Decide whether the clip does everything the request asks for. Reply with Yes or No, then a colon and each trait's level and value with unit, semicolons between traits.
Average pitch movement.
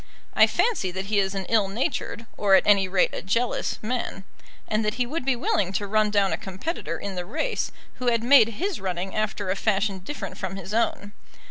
Yes: average, 3.4 semitones